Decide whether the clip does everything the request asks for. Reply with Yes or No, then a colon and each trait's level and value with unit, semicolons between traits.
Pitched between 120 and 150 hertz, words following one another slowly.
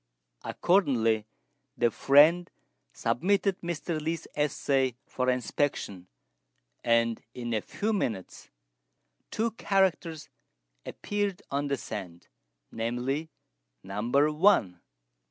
Yes: medium, 140 Hz; slow, 90 wpm